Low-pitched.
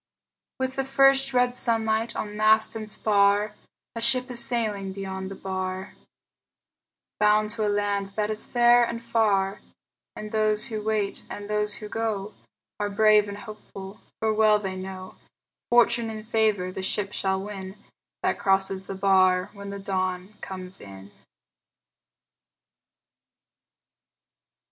No: high, 210 Hz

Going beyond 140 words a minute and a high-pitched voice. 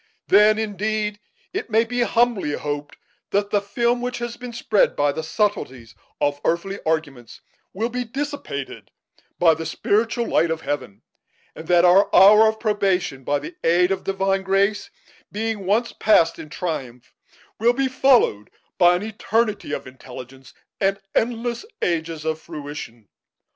Yes: average, 150 wpm; high, 195 Hz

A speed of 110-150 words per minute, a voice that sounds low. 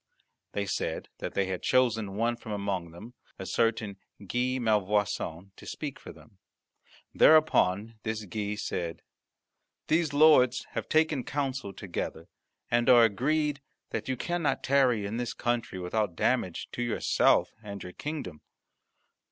Yes: average, 140 wpm; low, 110 Hz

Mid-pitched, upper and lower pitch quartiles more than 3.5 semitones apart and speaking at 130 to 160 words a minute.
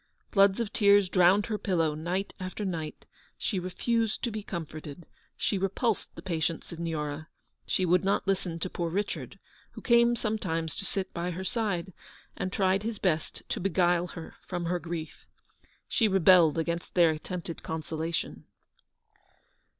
No: medium, 180 Hz; average, 3.1 semitones; average, 155 wpm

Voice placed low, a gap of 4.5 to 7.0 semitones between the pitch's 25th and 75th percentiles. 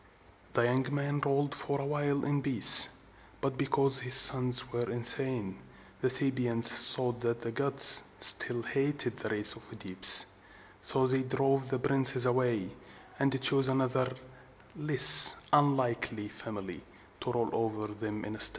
No: low, 130 Hz; average, 2.7 semitones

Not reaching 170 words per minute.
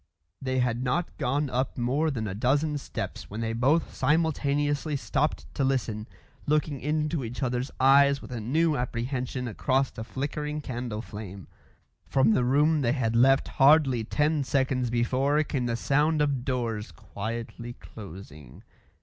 Yes: average, 150 wpm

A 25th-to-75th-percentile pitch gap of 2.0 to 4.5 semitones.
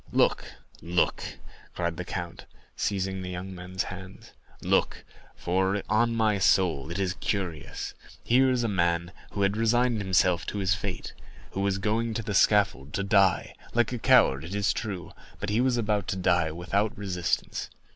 Yes: average, 3.0 semitones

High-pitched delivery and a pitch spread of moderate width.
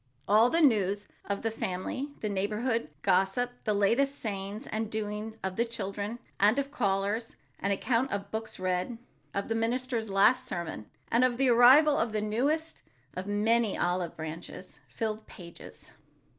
Yes: high, 215 Hz; average, 3.5 semitones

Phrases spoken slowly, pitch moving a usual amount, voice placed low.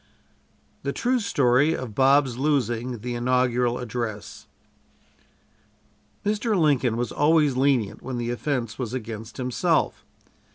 Yes: slow, 115 wpm; average, 3.0 semitones; low, 125 Hz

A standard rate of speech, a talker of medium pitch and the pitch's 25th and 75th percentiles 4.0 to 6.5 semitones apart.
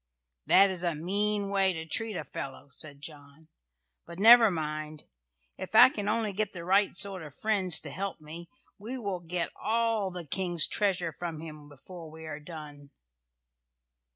Yes: average, 170 wpm; medium, 175 Hz; average, 4.5 semitones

